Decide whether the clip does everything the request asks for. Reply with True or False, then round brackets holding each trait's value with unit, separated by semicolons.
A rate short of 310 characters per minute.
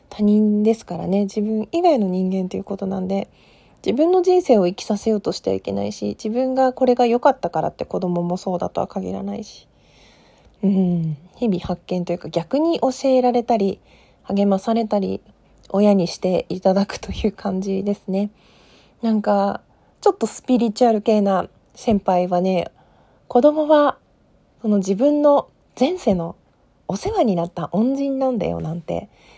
False (320 characters per minute)